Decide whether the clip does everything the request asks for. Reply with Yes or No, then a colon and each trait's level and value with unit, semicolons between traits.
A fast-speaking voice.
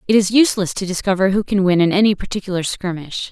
Yes: fast, 215 wpm